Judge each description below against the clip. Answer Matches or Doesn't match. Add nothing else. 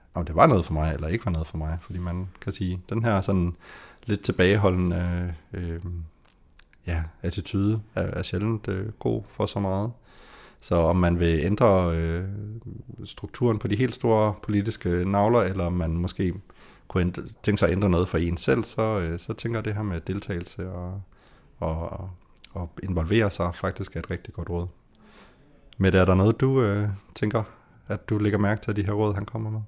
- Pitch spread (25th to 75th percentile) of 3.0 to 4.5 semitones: Matches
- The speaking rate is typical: Matches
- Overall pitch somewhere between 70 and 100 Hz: Matches